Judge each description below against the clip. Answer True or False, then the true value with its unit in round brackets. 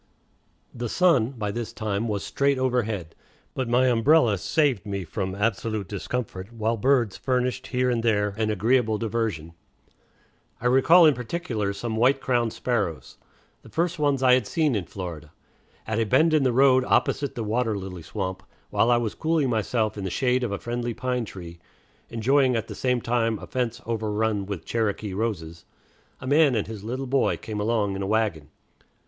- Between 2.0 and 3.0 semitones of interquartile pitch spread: False (3.7 semitones)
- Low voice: True (115 Hz)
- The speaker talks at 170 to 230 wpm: True (180 wpm)